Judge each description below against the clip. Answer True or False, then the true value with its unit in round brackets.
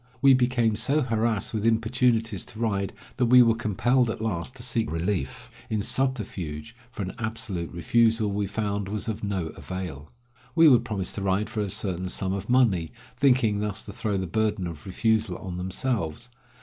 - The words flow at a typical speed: True (180 wpm)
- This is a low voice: True (110 Hz)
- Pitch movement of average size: True (3.8 semitones)